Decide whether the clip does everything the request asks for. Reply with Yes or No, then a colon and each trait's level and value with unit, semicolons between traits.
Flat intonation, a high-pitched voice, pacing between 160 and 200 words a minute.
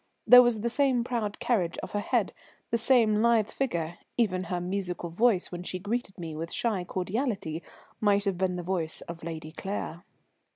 No: average, 4.8 semitones; high, 195 Hz; average, 180 wpm